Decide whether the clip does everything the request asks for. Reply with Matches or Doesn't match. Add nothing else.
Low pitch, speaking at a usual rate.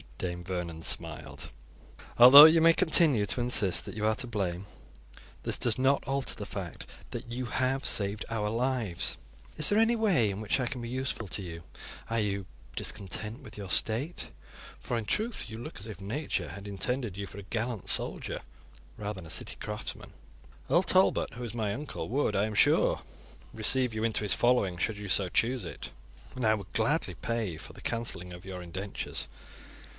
Matches